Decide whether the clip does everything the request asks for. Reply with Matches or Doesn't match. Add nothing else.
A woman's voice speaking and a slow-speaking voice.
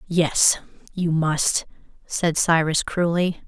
Matches